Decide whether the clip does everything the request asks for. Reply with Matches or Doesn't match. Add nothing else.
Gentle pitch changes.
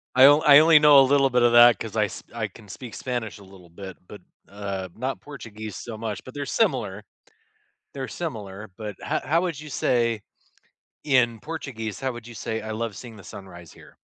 Doesn't match